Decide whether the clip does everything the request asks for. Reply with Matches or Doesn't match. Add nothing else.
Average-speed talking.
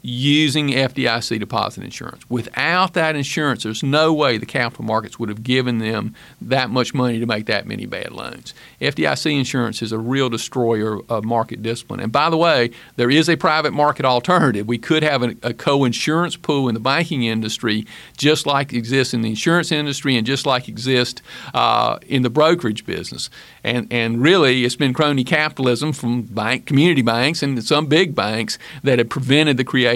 Matches